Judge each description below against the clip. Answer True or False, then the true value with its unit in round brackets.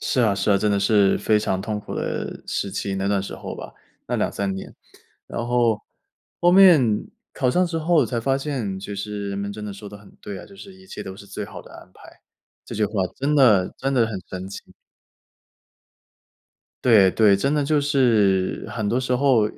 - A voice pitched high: False (105 Hz)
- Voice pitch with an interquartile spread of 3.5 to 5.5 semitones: True (5.1 semitones)